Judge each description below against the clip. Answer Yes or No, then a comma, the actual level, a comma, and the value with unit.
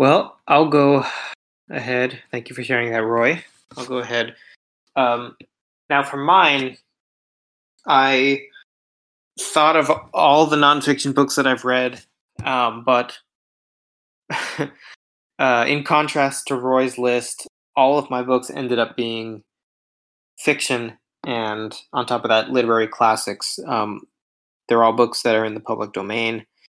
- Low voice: Yes, low, 125 Hz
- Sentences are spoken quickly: No, slow, 135 wpm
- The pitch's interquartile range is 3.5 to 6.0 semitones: No, average, 2.8 semitones